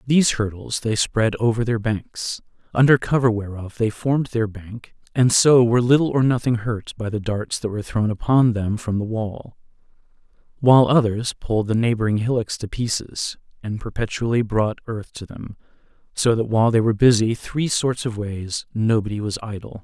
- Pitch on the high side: No, low, 115 Hz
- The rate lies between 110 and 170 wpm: No, average, 180 wpm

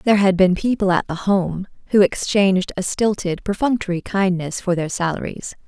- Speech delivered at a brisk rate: No, average, 170 wpm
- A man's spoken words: No, female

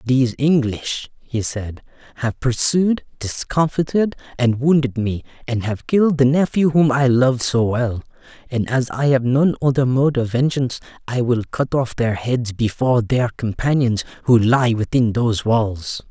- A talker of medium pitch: No, low, 125 Hz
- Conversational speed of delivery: Yes, average, 160 wpm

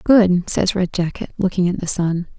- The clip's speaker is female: Yes, female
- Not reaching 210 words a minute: Yes, average, 200 wpm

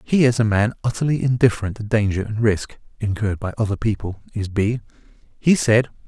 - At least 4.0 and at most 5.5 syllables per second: No, 5.9 syllables/s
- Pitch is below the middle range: Yes, low, 110 Hz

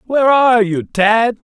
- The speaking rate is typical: Yes, average, 160 wpm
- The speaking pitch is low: No, high, 220 Hz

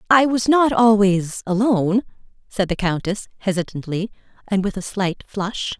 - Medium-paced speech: Yes, average, 145 wpm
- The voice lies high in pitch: Yes, high, 200 Hz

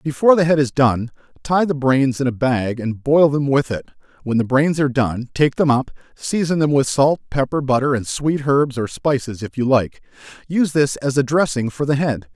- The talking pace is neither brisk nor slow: No, fast, 220 wpm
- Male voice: Yes, male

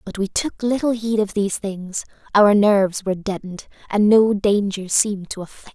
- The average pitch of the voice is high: Yes, high, 205 Hz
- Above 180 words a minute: Yes, average, 200 wpm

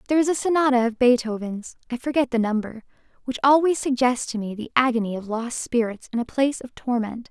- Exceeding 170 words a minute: Yes, fast, 205 wpm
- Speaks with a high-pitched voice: Yes, high, 245 Hz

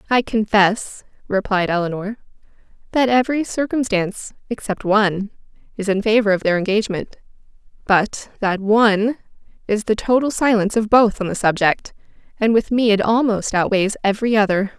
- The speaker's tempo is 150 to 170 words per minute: No, average, 140 wpm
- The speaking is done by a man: No, female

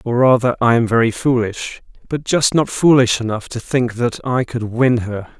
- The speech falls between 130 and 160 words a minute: No, average, 200 wpm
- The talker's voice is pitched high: No, low, 120 Hz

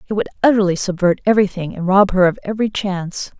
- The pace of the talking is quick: No, average, 195 wpm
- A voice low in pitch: No, high, 190 Hz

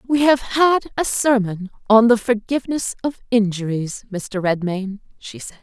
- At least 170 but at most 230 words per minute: No, average, 150 wpm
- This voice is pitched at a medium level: No, high, 225 Hz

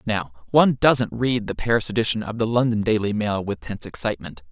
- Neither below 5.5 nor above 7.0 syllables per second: Yes, 6.0 syllables/s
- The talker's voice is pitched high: No, low, 110 Hz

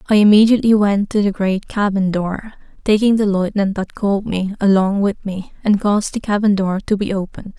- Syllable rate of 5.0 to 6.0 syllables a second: Yes, 5.7 syllables/s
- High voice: Yes, high, 200 Hz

